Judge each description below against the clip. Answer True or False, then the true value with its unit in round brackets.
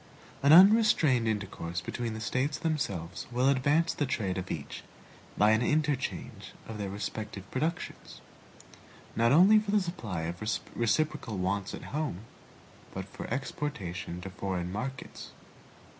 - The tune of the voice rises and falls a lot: True (7.7 semitones)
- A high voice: False (115 Hz)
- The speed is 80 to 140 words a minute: True (135 wpm)